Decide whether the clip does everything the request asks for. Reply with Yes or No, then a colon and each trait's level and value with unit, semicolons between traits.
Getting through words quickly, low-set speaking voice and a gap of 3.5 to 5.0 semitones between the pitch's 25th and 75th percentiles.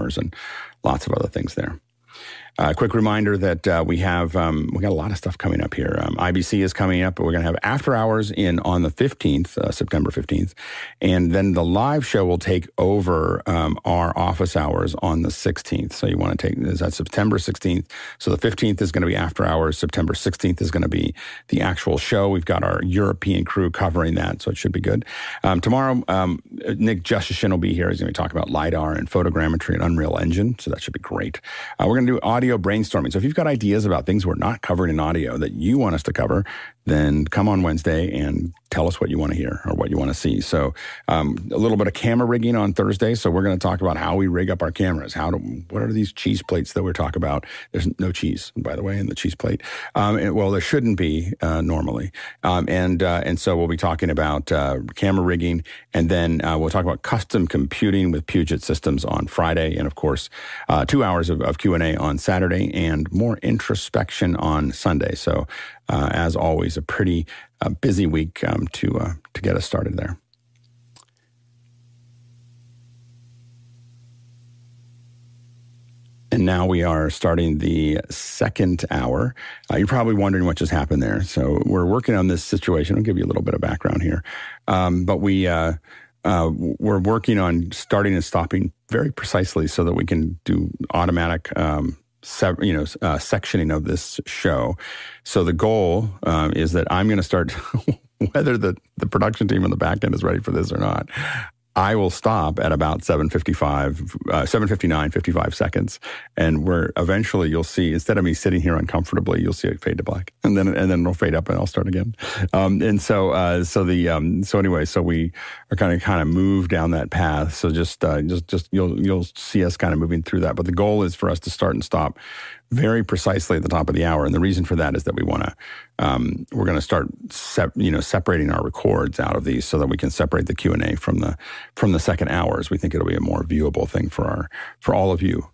Yes: fast, 225 wpm; very low, 90 Hz; average, 3.8 semitones